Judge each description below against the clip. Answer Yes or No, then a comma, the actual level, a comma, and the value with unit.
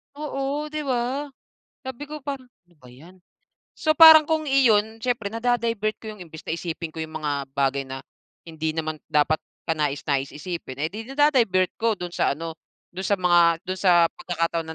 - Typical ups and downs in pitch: No, wide, 7.9 semitones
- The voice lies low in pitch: No, medium, 185 Hz